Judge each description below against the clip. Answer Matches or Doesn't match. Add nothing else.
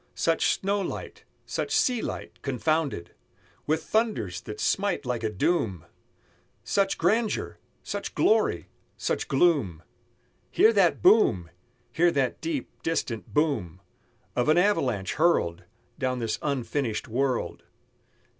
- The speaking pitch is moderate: Matches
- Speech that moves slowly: Matches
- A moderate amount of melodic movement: Doesn't match